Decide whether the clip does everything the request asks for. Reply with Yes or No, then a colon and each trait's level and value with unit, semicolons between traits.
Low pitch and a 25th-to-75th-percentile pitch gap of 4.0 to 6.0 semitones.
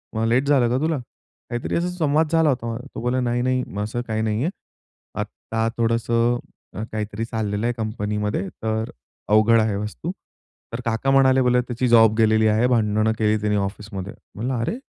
No: low, 115 Hz; narrow, 2.5 semitones